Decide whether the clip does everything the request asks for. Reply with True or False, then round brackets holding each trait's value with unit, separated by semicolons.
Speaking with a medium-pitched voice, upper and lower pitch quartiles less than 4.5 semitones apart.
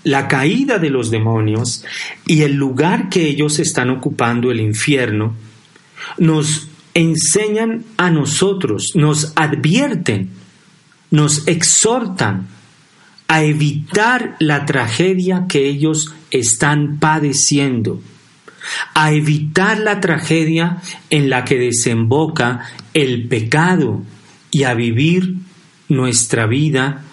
False (150 Hz; 4.9 semitones)